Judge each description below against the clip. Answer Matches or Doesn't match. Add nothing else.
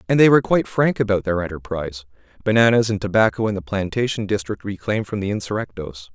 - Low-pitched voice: Matches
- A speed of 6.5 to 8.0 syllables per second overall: Matches